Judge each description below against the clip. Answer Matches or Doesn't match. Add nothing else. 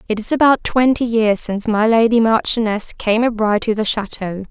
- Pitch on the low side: Doesn't match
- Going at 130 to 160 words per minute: Doesn't match